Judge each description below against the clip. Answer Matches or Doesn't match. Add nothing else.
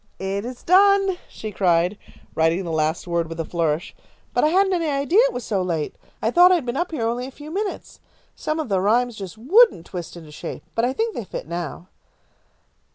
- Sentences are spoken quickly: Matches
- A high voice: Matches